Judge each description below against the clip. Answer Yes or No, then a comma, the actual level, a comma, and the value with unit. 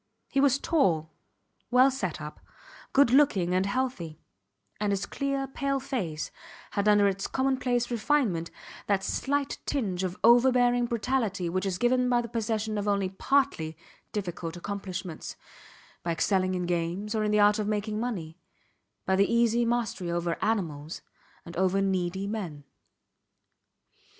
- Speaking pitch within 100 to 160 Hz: No, high, 205 Hz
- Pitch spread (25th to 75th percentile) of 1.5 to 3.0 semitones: No, average, 5.1 semitones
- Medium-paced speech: Yes, average, 145 wpm